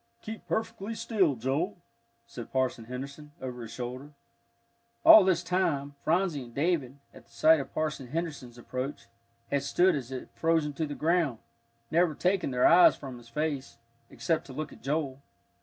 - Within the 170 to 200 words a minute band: No, average, 160 wpm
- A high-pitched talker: No, medium, 145 Hz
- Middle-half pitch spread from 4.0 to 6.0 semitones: Yes, average, 4.4 semitones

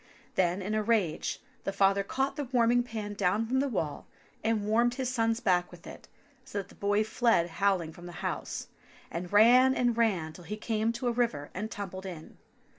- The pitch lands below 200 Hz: No, high, 215 Hz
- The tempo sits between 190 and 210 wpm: Yes, average, 200 wpm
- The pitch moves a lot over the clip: No, average, 4.1 semitones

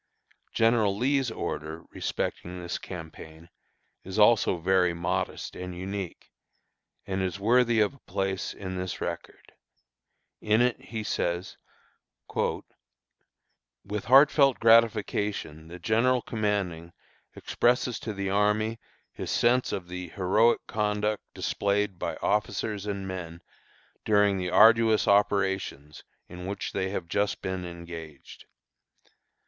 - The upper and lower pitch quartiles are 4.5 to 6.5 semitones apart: No, average, 3.4 semitones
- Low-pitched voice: Yes, low, 100 Hz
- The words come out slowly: Yes, slow, 115 wpm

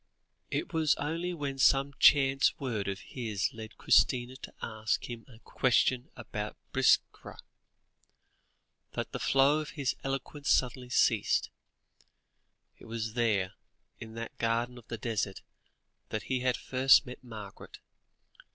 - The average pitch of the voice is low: Yes, low, 125 Hz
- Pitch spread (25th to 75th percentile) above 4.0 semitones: No, average, 3.3 semitones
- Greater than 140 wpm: No, slow, 135 wpm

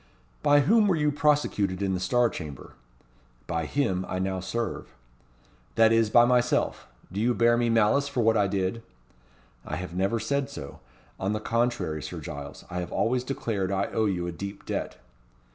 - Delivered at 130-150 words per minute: No, average, 180 wpm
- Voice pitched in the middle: No, low, 110 Hz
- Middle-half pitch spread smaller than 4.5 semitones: No, average, 4.8 semitones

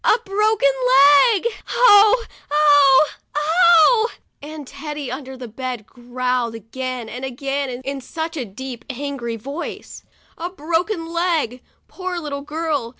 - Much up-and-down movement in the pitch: No, average, 4.6 semitones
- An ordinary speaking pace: No, slow, 125 wpm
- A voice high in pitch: Yes, very high, 280 Hz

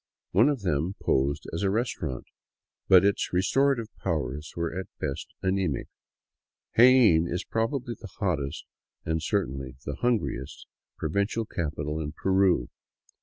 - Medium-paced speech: No, slow, 125 wpm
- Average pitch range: No, wide, 6.7 semitones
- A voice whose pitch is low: Yes, very low, 95 Hz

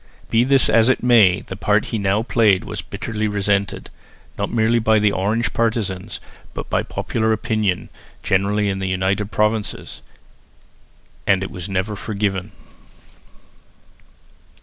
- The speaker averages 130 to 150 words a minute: Yes, average, 140 wpm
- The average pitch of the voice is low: Yes, low, 105 Hz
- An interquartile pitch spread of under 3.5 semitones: Yes, narrow, 2.4 semitones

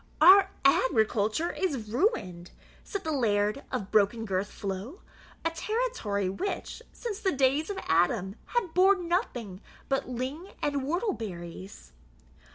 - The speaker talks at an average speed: No, slow, 130 wpm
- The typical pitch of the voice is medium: No, very high, 260 Hz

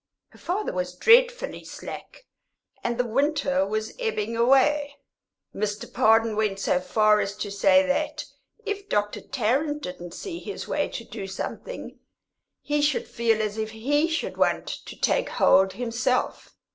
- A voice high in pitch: Yes, high, 235 Hz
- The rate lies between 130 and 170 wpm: Yes, average, 150 wpm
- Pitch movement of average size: No, wide, 5.8 semitones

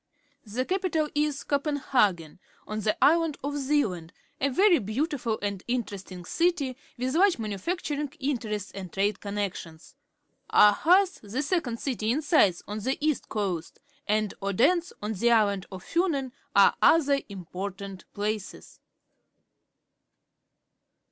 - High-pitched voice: Yes, high, 235 Hz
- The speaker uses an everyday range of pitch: No, wide, 6.6 semitones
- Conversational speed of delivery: No, slow, 130 wpm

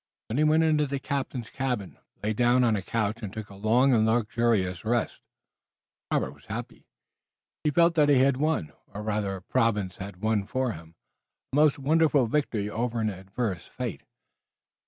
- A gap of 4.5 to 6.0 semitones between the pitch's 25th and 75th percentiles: Yes, average, 4.8 semitones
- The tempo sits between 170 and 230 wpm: Yes, average, 175 wpm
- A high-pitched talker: No, low, 115 Hz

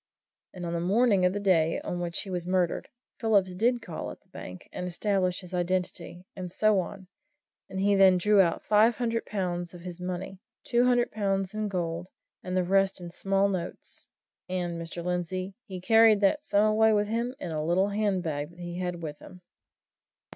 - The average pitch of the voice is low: No, medium, 185 Hz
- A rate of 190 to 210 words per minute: Yes, average, 195 wpm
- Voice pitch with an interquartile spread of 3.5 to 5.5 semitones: No, average, 2.7 semitones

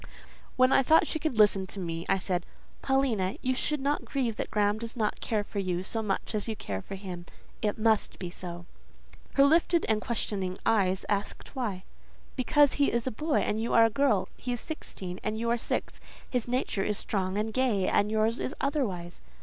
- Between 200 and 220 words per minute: Yes, fast, 205 wpm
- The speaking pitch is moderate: No, high, 215 Hz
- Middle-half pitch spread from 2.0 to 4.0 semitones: No, average, 4.8 semitones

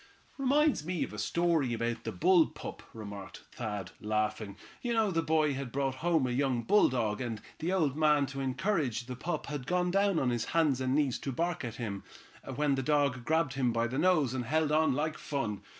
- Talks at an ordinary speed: No, fast, 210 wpm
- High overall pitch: No, medium, 140 Hz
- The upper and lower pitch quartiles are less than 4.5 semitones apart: No, average, 5.2 semitones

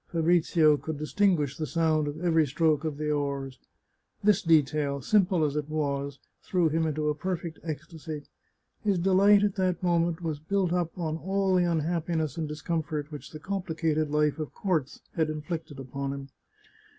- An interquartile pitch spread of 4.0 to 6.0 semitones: No, narrow, 2.6 semitones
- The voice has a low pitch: No, medium, 160 Hz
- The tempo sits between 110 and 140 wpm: No, average, 165 wpm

